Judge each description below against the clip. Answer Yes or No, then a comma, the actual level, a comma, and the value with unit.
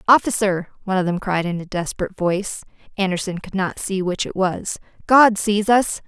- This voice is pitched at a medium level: No, high, 195 Hz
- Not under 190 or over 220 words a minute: No, average, 170 wpm